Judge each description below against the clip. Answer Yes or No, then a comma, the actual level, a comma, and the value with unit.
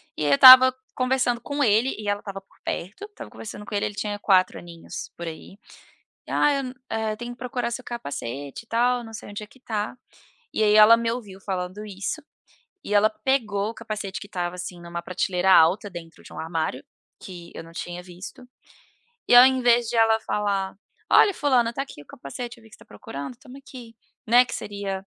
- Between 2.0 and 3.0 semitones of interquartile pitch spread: No, average, 4.6 semitones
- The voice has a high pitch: Yes, high, 210 Hz